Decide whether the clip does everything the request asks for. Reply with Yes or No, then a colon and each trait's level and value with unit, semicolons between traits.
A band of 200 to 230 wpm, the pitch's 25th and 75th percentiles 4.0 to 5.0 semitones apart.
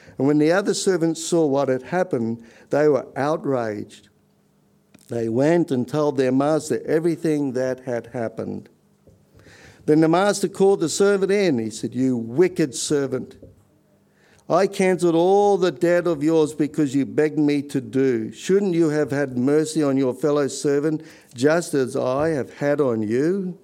No: average, 160 wpm; average, 4.6 semitones